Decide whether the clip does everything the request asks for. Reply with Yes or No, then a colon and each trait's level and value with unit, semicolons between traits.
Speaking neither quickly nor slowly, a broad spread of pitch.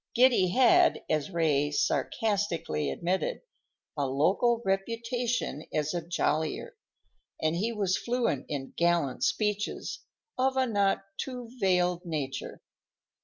No: slow, 115 wpm; wide, 7.0 semitones